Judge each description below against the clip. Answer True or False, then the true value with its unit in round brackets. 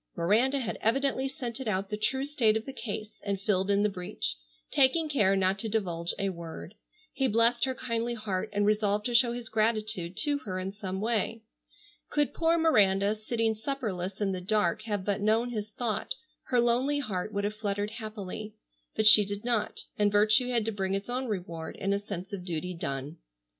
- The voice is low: False (215 Hz)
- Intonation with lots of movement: False (3.4 semitones)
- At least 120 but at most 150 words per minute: False (195 wpm)